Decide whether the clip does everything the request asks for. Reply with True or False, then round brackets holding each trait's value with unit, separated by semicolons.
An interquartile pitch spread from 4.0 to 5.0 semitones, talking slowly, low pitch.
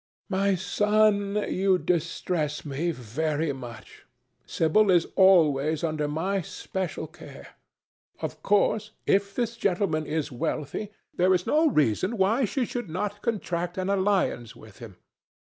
False (4.6 semitones; 130 wpm; 180 Hz)